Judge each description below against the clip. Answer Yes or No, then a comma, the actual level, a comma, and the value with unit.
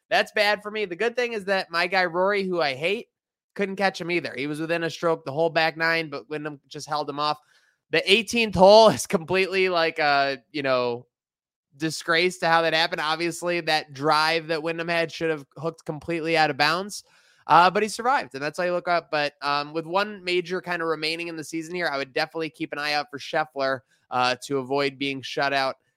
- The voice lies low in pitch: No, medium, 165 Hz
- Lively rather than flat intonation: No, average, 3.5 semitones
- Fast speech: Yes, fast, 225 wpm